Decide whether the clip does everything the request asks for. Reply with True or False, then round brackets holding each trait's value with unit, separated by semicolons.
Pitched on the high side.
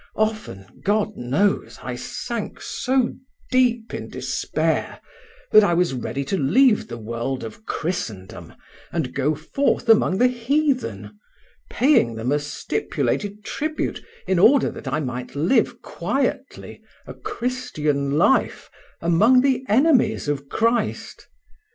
True (200 Hz)